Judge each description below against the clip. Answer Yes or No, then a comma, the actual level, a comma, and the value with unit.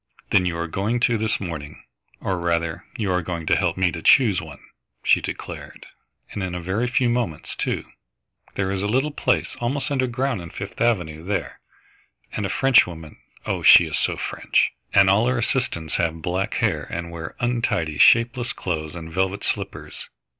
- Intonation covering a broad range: Yes, wide, 6.0 semitones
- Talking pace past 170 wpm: Yes, average, 180 wpm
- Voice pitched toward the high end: No, very low, 95 Hz